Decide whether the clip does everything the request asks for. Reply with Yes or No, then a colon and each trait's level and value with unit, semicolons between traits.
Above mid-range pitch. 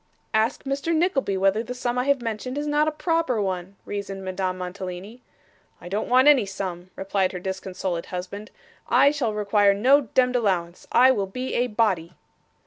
Yes: high, 210 Hz